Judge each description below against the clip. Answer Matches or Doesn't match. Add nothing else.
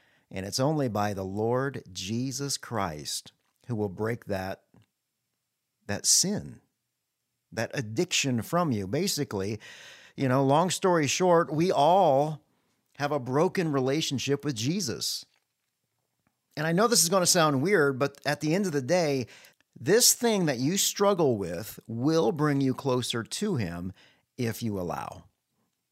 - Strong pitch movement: Matches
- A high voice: Doesn't match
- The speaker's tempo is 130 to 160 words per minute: Matches